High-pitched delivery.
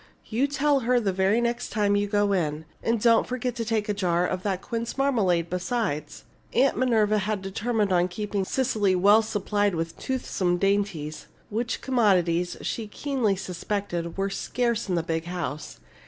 Yes: high, 205 Hz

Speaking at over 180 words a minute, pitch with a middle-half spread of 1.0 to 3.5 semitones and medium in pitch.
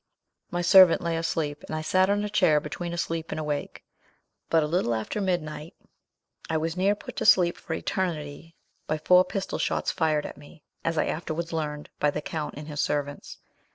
Yes: average, 190 wpm; average, 2.8 semitones; medium, 165 Hz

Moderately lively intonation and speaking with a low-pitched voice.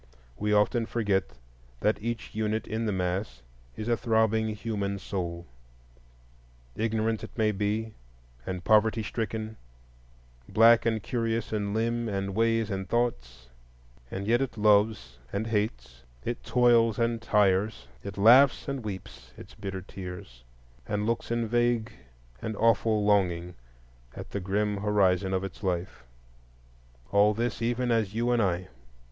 Yes: average, 3.1 semitones; low, 105 Hz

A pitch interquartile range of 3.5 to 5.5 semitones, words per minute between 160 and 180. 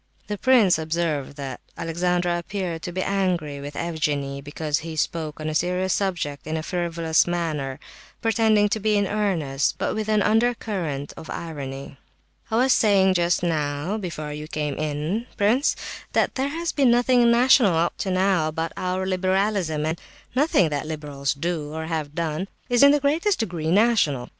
Yes: average, 5.2 semitones; average, 170 wpm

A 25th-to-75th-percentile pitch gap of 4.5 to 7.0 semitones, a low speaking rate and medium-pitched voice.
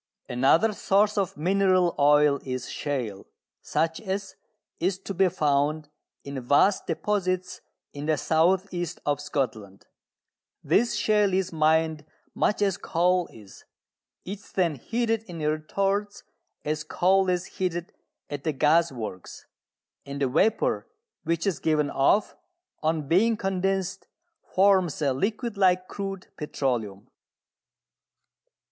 Yes: average, 4.8 semitones; slow, 125 wpm; medium, 170 Hz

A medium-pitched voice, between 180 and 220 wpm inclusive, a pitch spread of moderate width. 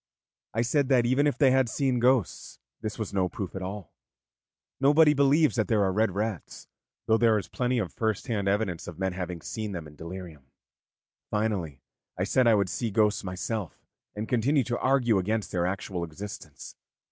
No: low, 110 Hz; average, 185 wpm; average, 4.7 semitones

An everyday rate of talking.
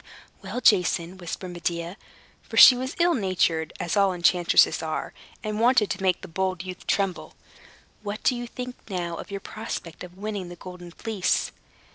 Yes: average, 170 wpm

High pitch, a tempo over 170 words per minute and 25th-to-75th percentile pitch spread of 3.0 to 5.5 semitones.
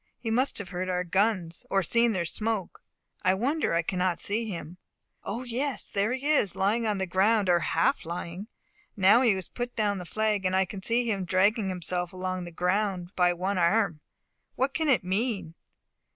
Yes: high, 195 Hz; average, 195 wpm; average, 3.8 semitones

